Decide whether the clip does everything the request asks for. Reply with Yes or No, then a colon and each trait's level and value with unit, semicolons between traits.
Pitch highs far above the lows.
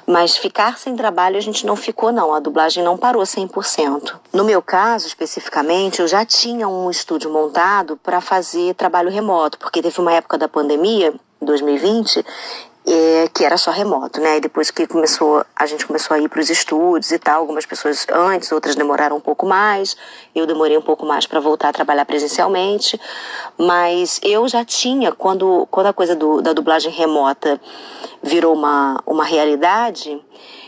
No: average, 3.8 semitones